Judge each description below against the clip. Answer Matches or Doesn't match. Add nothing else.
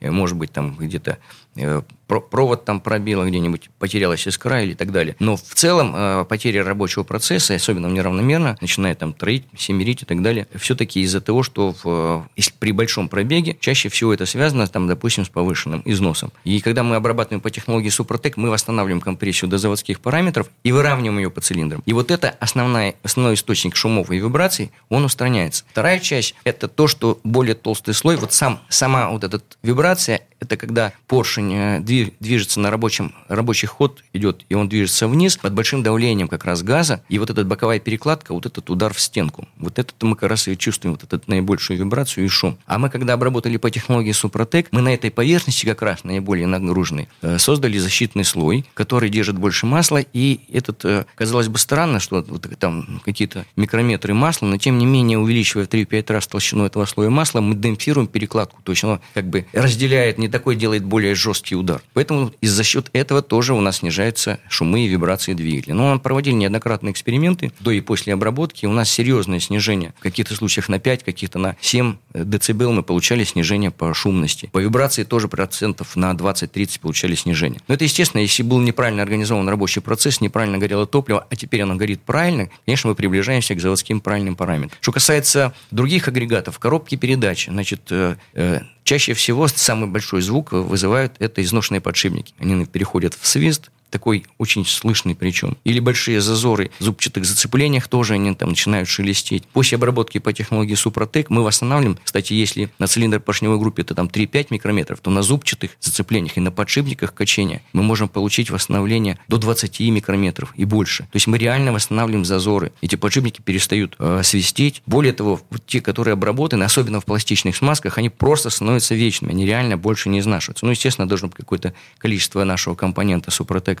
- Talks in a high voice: Doesn't match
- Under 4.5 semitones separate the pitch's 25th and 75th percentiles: Matches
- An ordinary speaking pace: Doesn't match